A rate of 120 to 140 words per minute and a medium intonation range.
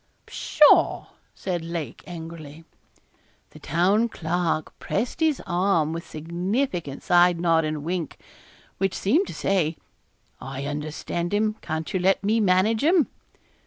Yes: slow, 135 wpm; average, 3.7 semitones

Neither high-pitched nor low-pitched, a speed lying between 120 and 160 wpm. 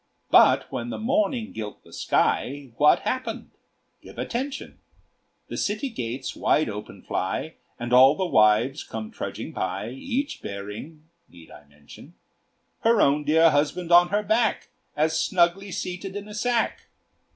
Yes: medium, 160 Hz; average, 145 wpm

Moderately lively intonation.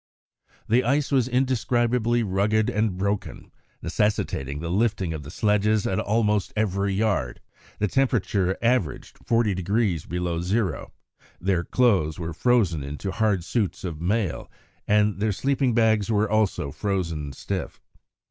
Yes: average, 4.2 semitones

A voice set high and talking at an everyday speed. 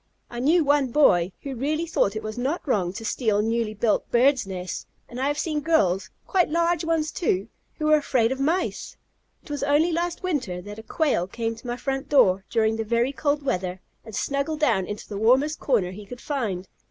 No: very high, 255 Hz; fast, 210 wpm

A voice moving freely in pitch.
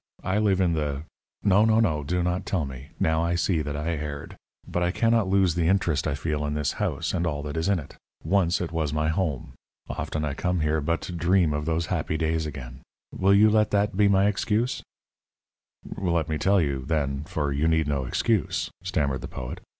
No: average, 4.0 semitones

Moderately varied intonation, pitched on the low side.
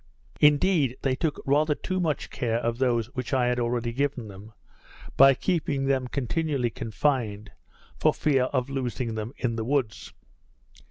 Yes: average, 3.4 semitones; low, 130 Hz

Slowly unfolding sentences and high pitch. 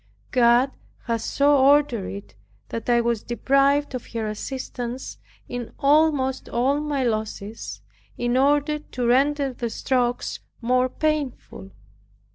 Yes: slow, 120 wpm; very high, 255 Hz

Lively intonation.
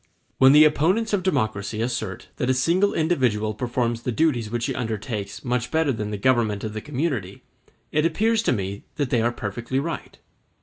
Yes: wide, 6.0 semitones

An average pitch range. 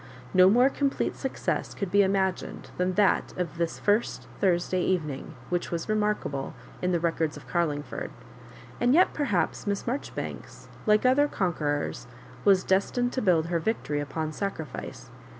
Yes: average, 4.3 semitones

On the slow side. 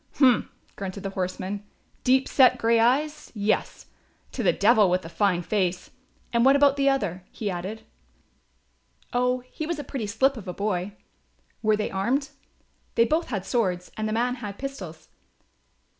No: average, 165 wpm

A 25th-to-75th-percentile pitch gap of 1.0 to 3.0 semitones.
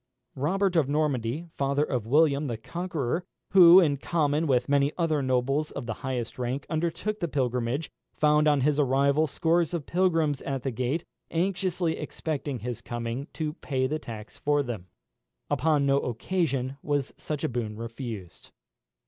No: average, 4.1 semitones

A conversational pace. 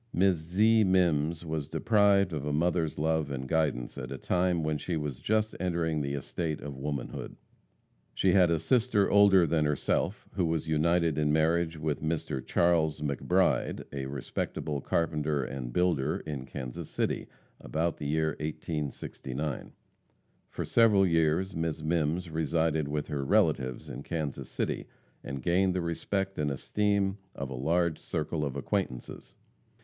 Yes: average, 150 wpm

